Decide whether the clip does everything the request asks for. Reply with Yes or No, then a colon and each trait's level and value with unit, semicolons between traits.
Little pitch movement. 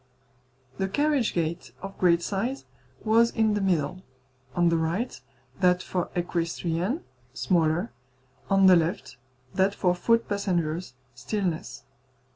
No: average, 3.3 semitones